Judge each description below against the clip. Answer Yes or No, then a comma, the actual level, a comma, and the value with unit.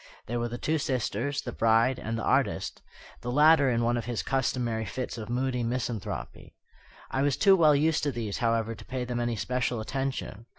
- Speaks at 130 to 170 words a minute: No, average, 200 wpm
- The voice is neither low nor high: No, low, 120 Hz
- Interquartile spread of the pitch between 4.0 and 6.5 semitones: No, narrow, 2.6 semitones